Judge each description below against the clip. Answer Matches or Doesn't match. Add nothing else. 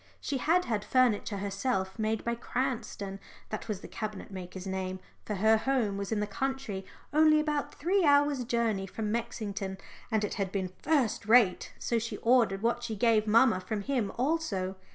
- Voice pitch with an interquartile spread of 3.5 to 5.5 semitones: Matches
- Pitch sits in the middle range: Doesn't match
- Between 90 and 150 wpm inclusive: Doesn't match